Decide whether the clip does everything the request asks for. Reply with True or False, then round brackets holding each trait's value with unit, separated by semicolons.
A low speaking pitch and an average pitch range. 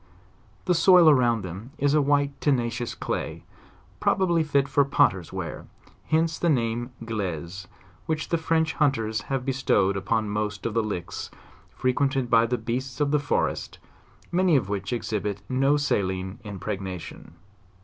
False (120 Hz; 5.8 semitones)